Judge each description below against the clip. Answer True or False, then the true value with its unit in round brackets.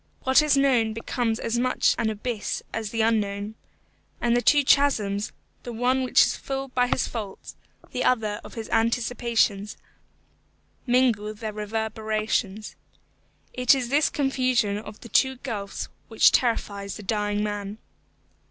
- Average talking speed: True (145 wpm)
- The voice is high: True (225 Hz)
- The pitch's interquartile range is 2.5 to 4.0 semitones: True (3.1 semitones)